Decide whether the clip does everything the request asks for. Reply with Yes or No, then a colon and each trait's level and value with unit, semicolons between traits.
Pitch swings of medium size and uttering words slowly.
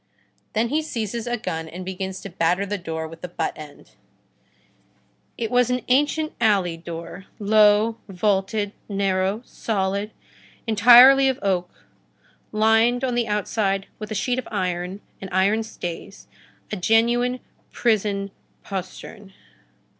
Yes: average, 3.5 semitones; slow, 130 wpm